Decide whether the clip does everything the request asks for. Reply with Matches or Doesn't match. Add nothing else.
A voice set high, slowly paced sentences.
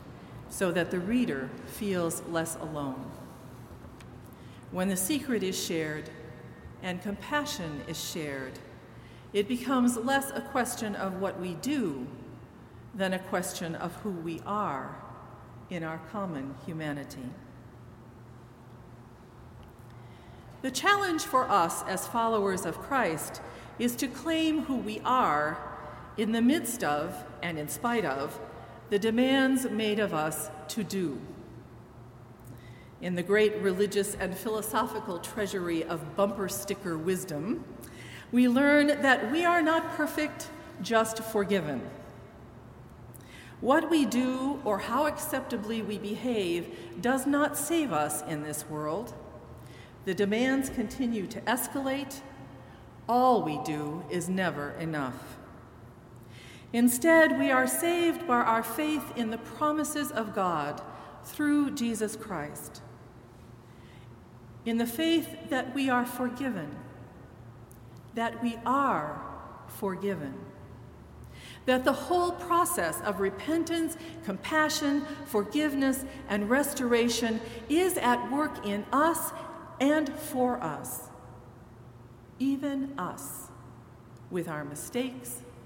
Matches